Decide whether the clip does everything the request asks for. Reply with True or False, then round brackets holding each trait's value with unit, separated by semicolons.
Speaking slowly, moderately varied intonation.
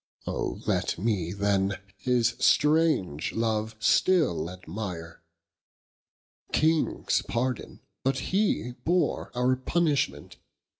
False (90 wpm; 7.6 semitones)